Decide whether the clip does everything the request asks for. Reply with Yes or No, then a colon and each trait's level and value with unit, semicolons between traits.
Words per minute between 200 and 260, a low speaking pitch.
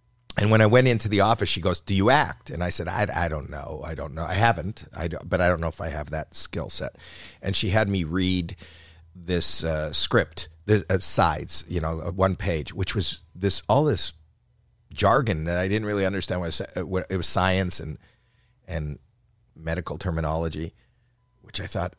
Yes: fast, 205 wpm; very low, 90 Hz